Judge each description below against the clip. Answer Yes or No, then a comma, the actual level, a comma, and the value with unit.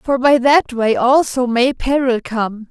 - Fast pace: No, average, 175 wpm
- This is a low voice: No, very high, 255 Hz